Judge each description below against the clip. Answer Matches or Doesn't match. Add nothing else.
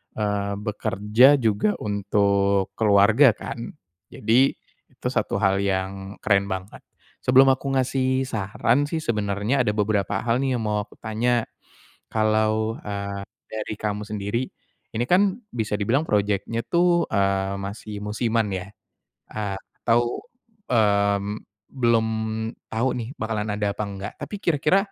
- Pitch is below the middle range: Matches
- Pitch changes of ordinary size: Matches